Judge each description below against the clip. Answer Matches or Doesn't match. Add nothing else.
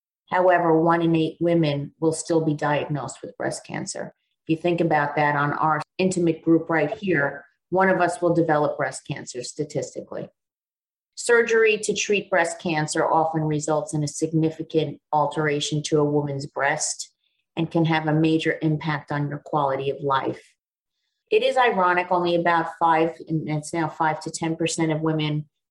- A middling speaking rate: Matches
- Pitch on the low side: Doesn't match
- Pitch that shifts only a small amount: Matches